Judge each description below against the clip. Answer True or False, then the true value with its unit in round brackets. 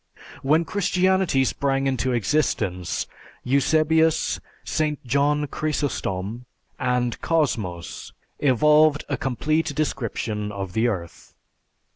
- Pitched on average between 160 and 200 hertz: False (135 Hz)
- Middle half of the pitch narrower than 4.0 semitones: False (4.9 semitones)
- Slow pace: True (90 wpm)